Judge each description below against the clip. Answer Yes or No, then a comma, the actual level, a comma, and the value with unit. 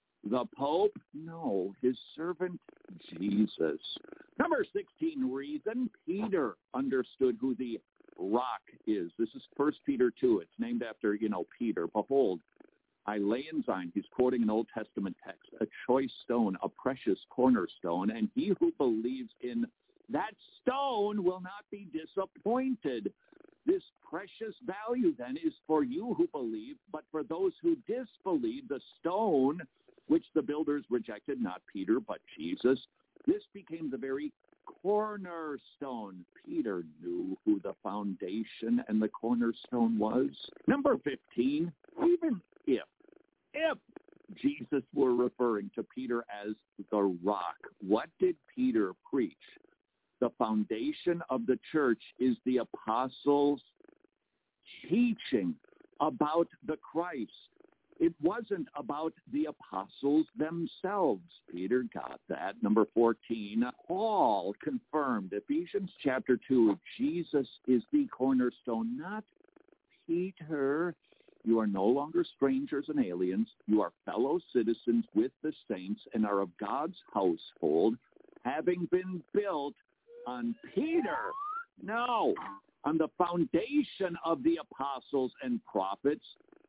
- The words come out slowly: Yes, slow, 120 wpm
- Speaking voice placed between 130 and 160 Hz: No, medium, 185 Hz